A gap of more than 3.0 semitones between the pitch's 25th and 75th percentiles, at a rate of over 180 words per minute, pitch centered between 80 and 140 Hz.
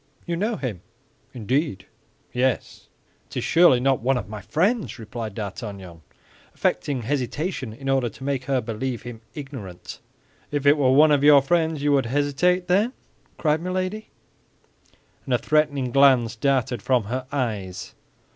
No: average, 4.2 semitones; average, 150 wpm; low, 135 Hz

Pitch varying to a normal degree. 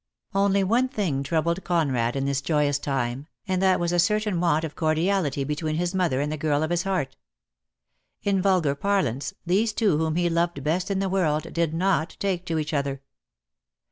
Yes: average, 4.3 semitones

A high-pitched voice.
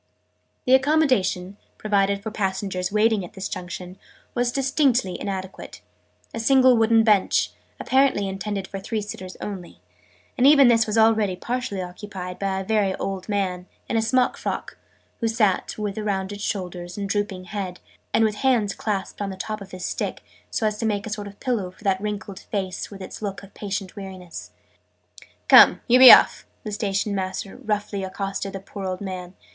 Yes: high, 200 Hz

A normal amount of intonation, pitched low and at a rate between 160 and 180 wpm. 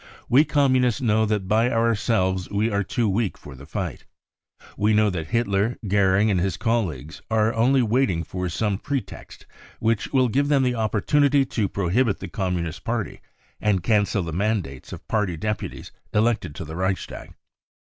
Yes: average, 3.8 semitones; low, 105 Hz; average, 170 wpm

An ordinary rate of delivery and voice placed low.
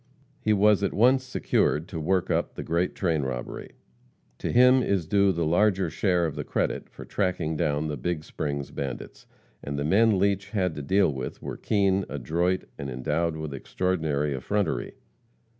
Yes: average, 175 wpm; very low, 85 Hz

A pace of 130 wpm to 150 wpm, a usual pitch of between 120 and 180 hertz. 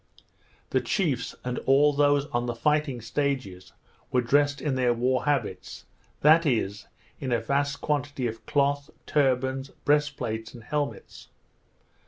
Yes: average, 140 wpm; low, 135 Hz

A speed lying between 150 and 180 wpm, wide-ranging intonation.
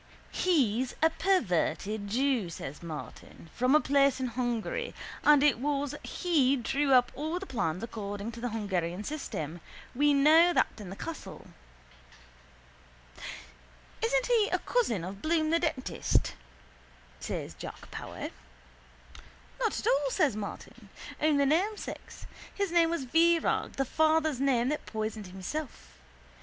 No: slow, 135 wpm; wide, 6.5 semitones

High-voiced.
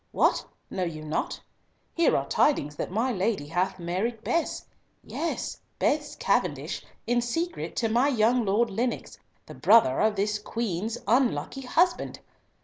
Yes: high, 225 Hz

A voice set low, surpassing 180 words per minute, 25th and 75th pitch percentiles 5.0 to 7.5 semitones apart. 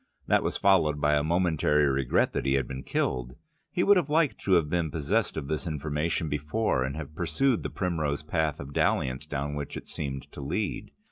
No: very low, 75 Hz; fast, 205 wpm; average, 3.6 semitones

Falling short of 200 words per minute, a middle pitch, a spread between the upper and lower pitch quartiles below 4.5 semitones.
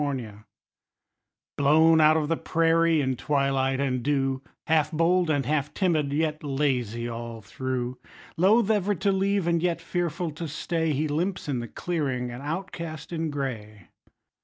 Yes: average, 155 wpm; medium, 150 Hz; average, 4.0 semitones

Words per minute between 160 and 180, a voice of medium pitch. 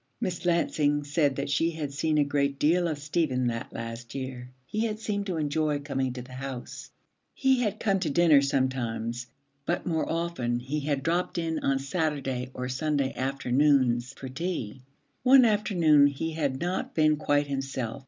Yes: average, 175 wpm; medium, 145 Hz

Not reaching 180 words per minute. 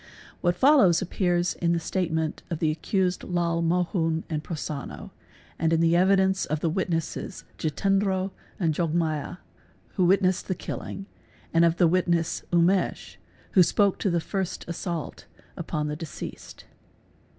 Yes: average, 145 wpm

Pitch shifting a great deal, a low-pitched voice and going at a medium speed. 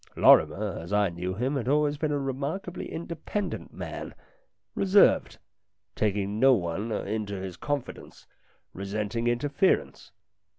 No: wide, 6.4 semitones; low, 115 Hz; slow, 120 wpm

